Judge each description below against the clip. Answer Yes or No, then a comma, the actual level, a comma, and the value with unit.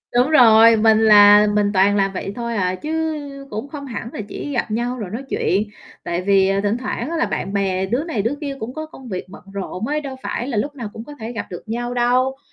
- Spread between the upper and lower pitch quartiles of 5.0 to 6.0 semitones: No, average, 4.4 semitones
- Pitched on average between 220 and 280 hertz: Yes, high, 225 Hz